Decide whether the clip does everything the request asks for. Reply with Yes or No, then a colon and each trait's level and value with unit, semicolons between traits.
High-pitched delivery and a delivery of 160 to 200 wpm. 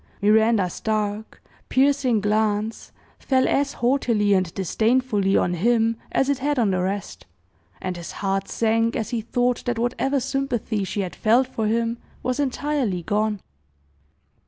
No: high, 225 Hz; average, 145 wpm